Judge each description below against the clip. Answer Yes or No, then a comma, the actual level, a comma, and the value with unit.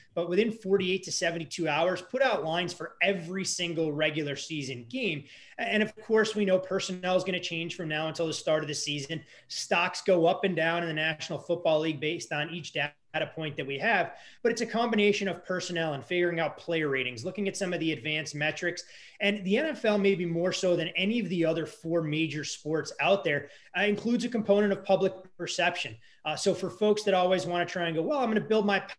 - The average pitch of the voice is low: No, medium, 175 Hz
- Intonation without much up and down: No, average, 3.8 semitones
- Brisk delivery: Yes, fast, 225 wpm